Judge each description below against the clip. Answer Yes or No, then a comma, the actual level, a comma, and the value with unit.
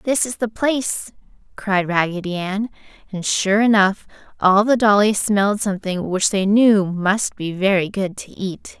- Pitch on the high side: Yes, high, 200 Hz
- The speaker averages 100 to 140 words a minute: No, average, 165 wpm